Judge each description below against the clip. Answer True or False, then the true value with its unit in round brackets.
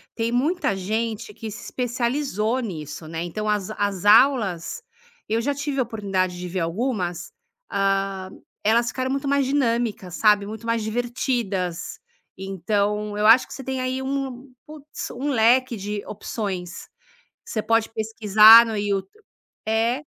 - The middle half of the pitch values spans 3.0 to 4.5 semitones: True (4.1 semitones)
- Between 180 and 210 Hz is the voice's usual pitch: False (220 Hz)